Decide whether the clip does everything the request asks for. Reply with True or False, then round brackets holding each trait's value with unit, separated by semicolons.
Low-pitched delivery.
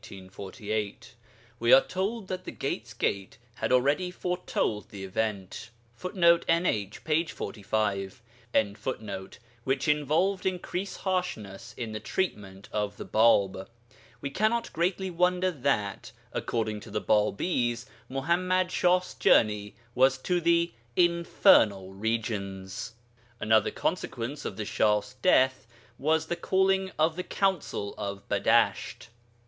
True (130 Hz)